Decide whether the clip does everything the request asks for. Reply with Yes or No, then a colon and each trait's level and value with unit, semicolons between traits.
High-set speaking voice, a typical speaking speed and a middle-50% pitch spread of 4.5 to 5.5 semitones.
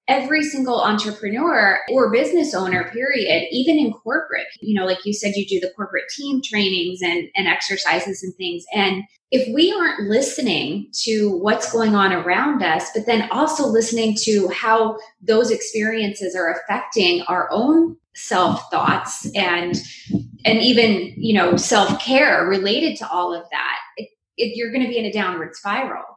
Yes: high, 220 Hz; average, 165 wpm; average, 5.0 semitones